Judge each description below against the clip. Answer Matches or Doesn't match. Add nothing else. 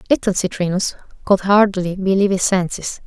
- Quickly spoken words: Doesn't match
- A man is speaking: Doesn't match